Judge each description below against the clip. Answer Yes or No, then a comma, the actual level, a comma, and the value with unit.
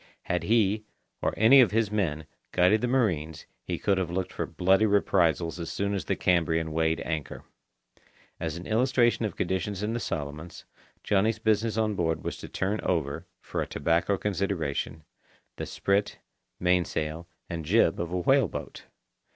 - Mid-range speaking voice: No, very low, 90 Hz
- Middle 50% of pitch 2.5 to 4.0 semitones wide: No, average, 4.5 semitones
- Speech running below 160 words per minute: No, average, 165 wpm